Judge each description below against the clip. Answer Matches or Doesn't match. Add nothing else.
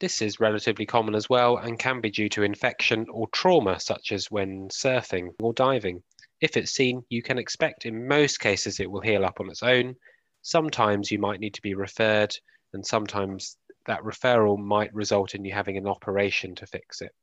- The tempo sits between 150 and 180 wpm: Doesn't match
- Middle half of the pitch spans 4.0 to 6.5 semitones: Doesn't match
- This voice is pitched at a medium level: Doesn't match